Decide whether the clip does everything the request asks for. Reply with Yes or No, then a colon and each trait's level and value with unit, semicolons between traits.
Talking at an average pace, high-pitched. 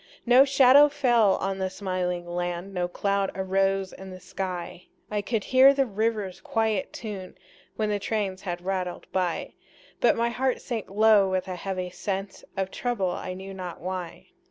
Yes: average, 170 wpm; high, 195 Hz